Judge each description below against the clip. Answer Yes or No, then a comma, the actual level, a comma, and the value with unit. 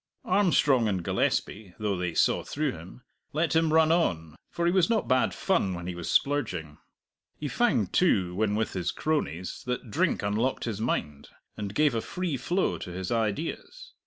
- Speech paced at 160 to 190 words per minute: Yes, average, 180 wpm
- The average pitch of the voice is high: No, low, 115 Hz